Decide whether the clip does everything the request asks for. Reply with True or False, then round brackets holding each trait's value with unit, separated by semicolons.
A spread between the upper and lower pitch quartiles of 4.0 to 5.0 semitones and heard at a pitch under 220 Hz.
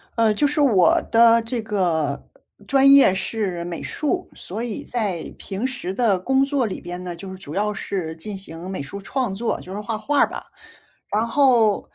True (4.7 semitones; 210 Hz)